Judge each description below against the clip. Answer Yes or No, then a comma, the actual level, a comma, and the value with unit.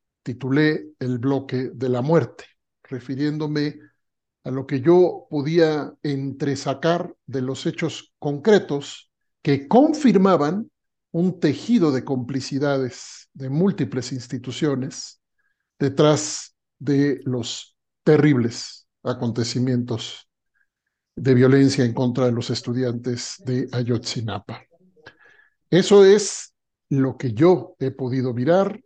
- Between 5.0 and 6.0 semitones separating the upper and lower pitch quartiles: No, average, 3.9 semitones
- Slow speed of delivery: Yes, slow, 100 wpm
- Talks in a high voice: No, medium, 140 Hz